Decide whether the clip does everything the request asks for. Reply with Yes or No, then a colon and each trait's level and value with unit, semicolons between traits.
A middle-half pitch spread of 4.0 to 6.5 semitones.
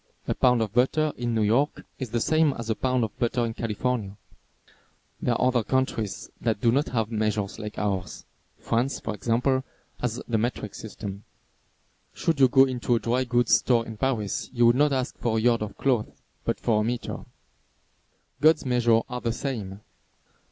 No: average, 2.7 semitones